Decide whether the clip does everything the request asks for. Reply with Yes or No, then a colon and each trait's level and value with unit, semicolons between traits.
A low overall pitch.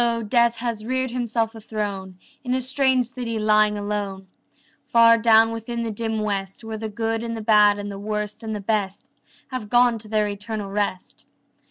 No: high, 220 Hz